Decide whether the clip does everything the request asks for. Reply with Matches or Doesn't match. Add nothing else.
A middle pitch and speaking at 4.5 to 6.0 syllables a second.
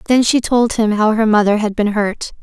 Doesn't match